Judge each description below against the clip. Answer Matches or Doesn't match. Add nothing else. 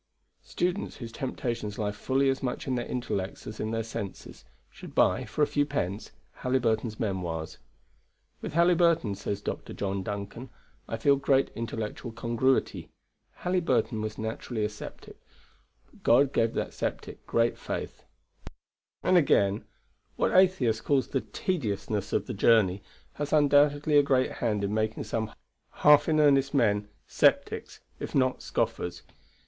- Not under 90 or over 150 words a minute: Matches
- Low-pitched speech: Matches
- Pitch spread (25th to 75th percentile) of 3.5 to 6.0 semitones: Matches